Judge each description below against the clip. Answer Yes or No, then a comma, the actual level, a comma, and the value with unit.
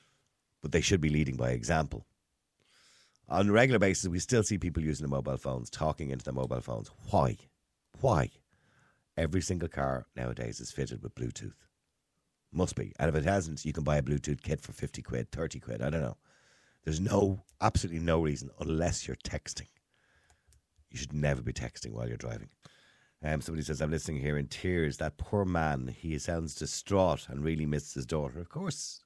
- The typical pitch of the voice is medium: No, very low, 75 Hz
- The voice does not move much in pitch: No, average, 3.7 semitones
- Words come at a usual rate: Yes, average, 190 wpm